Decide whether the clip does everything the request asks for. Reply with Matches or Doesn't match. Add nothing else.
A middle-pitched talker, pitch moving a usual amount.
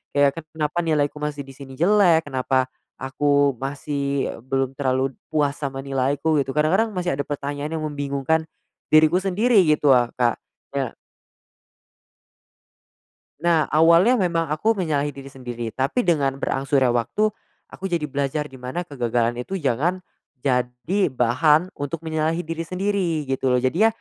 Matches